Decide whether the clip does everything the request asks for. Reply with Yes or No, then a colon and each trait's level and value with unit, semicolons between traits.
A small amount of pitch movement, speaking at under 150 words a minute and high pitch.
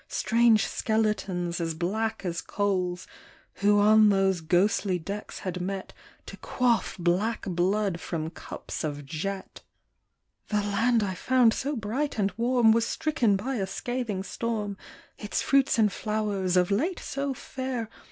No: average, 3.7 semitones; average, 140 wpm; high, 205 Hz